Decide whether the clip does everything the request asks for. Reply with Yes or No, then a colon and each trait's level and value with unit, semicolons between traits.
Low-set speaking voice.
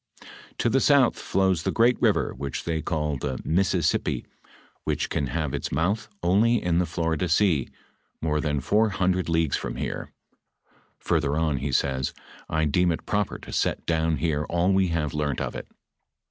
Yes: very low, 80 Hz